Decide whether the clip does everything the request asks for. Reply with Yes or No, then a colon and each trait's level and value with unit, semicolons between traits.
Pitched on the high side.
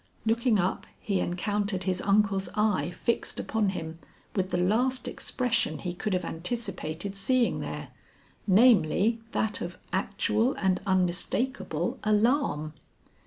Yes: high, 200 Hz